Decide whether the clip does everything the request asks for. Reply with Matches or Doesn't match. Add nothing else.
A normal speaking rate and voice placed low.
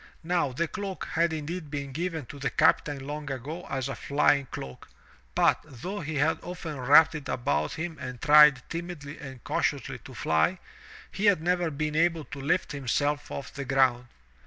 Doesn't match